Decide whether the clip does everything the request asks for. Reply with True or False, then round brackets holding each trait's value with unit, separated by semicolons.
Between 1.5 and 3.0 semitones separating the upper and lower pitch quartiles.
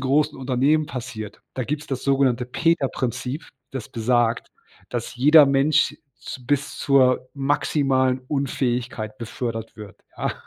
True (2.6 semitones)